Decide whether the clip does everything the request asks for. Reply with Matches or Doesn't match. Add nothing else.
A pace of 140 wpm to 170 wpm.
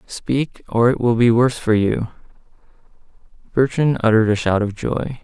Matches